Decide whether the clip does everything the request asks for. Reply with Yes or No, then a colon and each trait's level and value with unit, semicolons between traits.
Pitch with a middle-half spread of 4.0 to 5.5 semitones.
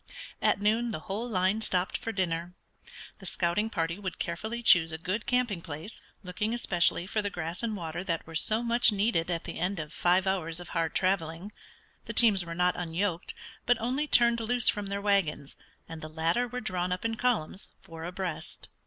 Yes: average, 4.7 semitones